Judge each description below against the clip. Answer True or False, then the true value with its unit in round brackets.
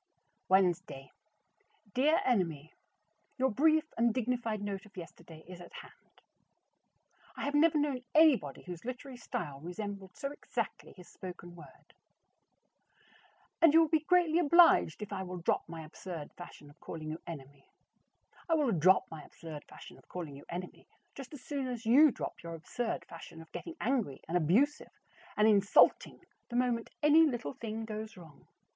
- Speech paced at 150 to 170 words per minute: True (160 wpm)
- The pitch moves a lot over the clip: True (7.9 semitones)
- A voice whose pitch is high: True (210 Hz)